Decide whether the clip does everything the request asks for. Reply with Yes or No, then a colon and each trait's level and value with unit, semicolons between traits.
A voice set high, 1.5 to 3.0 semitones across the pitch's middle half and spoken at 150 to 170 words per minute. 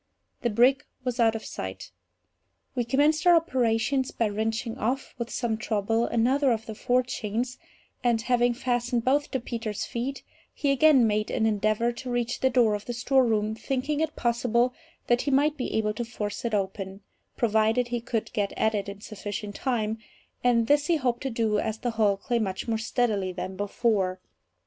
No: high, 235 Hz; average, 2.7 semitones; average, 180 wpm